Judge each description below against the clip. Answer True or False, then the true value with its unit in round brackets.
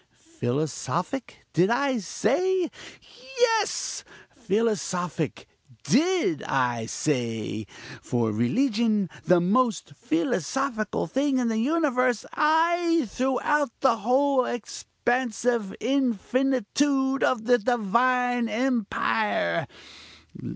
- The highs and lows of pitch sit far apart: True (5.8 semitones)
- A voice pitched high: True (245 Hz)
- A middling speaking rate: False (85 wpm)